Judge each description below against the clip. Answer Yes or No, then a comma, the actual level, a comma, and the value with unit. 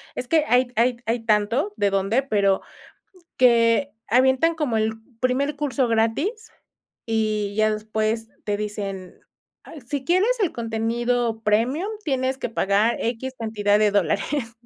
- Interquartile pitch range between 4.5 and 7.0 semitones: No, average, 3.6 semitones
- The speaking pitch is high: Yes, high, 230 Hz